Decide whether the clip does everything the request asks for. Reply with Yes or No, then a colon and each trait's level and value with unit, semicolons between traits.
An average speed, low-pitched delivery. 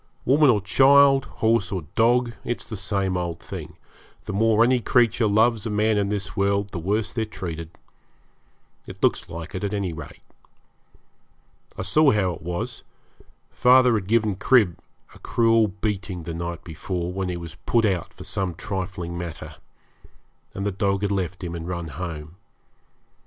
Yes: average, 170 wpm; low, 100 Hz